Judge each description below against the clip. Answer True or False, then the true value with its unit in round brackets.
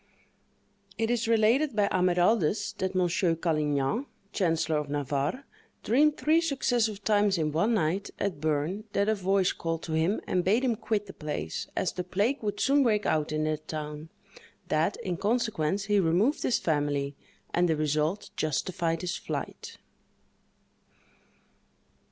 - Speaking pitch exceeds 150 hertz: True (185 Hz)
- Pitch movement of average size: False (5.7 semitones)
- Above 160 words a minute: False (150 wpm)